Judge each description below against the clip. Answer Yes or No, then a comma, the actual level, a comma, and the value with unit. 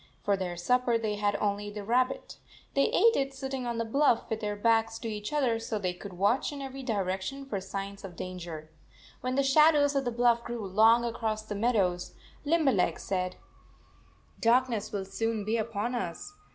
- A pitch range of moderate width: Yes, average, 4.0 semitones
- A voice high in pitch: Yes, high, 225 Hz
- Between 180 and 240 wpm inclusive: Yes, average, 190 wpm